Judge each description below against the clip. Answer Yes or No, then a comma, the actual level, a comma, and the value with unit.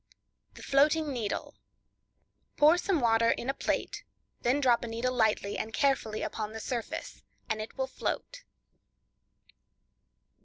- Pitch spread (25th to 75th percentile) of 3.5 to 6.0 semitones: Yes, average, 3.9 semitones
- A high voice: Yes, high, 245 Hz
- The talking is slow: Yes, slow, 125 wpm